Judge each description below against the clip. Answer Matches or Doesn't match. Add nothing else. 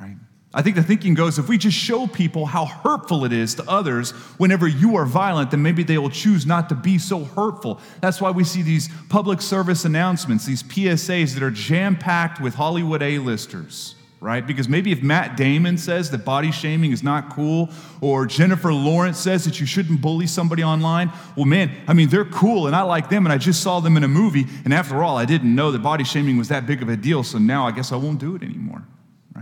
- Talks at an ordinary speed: Doesn't match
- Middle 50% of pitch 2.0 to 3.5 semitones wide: Doesn't match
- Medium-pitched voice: Matches